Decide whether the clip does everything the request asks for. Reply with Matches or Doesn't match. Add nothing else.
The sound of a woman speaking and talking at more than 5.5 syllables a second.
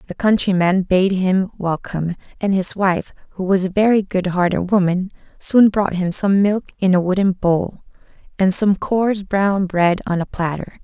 Doesn't match